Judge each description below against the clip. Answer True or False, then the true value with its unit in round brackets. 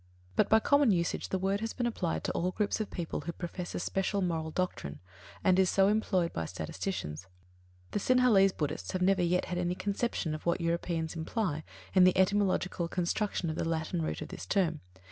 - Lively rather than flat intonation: False (2.9 semitones)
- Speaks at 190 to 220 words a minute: True (200 wpm)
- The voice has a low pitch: False (180 Hz)